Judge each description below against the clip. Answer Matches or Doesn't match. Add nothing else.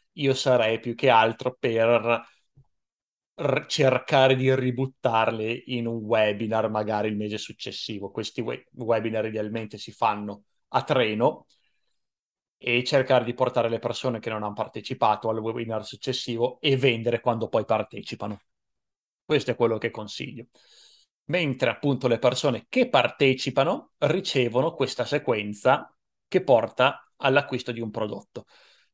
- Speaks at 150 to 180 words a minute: Doesn't match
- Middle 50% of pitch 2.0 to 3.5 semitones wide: Matches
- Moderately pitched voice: Doesn't match